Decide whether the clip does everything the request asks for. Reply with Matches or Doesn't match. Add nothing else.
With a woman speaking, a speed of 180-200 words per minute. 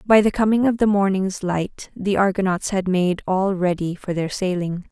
Matches